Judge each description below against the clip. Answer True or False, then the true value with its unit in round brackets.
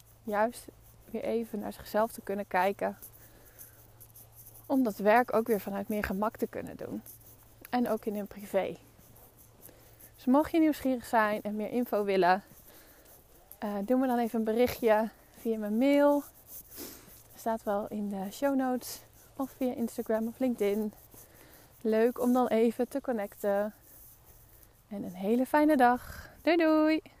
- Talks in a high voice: True (220 Hz)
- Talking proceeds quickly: False (150 wpm)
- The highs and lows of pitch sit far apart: False (4.0 semitones)